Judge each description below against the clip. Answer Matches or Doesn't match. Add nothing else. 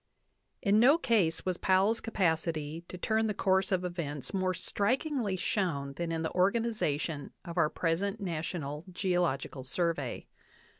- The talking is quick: Doesn't match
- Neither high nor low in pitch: Matches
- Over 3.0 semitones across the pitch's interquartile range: Matches